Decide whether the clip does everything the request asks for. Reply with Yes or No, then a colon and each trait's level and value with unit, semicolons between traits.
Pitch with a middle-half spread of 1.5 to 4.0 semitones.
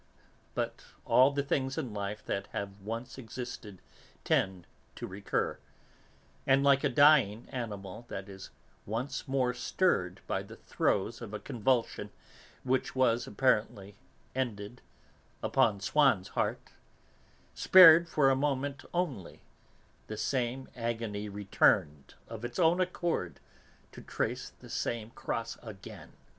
No: average, 4.7 semitones